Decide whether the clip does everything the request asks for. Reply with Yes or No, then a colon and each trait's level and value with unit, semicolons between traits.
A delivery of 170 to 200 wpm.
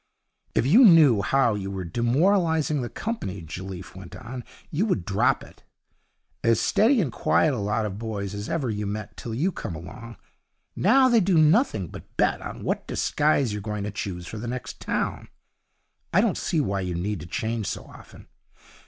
Yes: average, 190 wpm